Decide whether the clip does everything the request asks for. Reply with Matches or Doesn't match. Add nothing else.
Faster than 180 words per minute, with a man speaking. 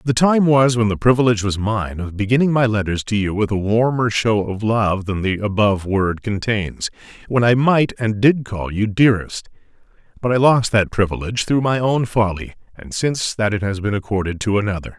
Matches